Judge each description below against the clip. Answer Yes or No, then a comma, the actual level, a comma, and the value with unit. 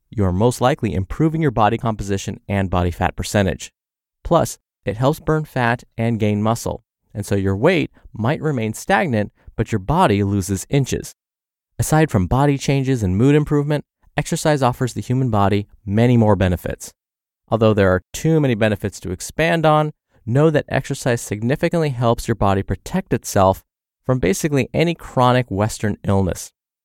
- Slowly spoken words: No, average, 160 wpm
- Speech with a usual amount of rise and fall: No, wide, 5.9 semitones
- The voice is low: Yes, low, 115 Hz